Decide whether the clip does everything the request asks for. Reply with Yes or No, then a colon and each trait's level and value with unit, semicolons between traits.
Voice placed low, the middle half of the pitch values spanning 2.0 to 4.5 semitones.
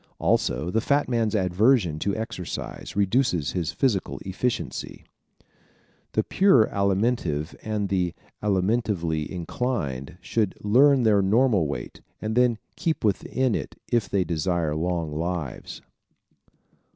No: low, 100 Hz; average, 5.2 semitones